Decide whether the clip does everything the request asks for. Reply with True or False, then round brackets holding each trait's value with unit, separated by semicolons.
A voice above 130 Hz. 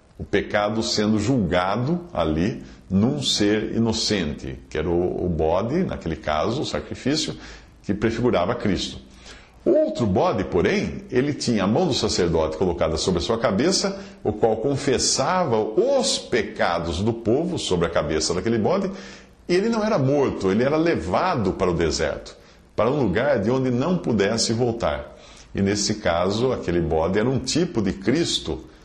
False (110 Hz)